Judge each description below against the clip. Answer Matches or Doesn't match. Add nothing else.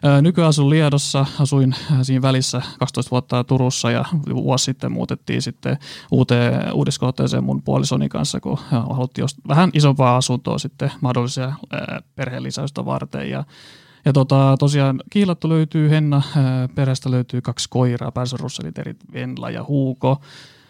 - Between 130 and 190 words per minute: Doesn't match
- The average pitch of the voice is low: Matches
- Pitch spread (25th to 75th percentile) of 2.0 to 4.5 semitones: Matches